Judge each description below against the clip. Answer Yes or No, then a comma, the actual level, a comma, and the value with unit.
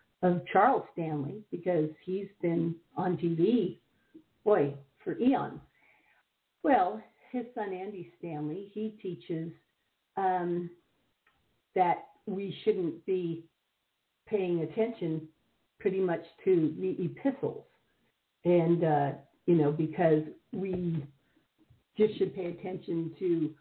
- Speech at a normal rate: No, slow, 105 wpm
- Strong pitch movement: No, average, 3.3 semitones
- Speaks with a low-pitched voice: No, medium, 175 Hz